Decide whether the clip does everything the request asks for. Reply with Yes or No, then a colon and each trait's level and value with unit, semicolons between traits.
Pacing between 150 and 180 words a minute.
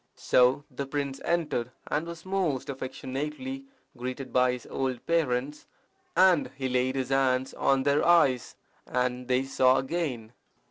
No: average, 140 wpm